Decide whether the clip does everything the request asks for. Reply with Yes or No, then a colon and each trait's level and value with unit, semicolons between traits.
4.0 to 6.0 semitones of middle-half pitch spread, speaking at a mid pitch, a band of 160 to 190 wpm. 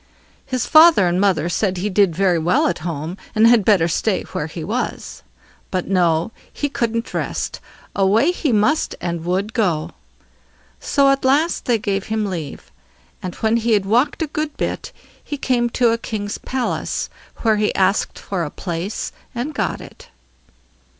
No: average, 5.1 semitones; high, 210 Hz; average, 170 wpm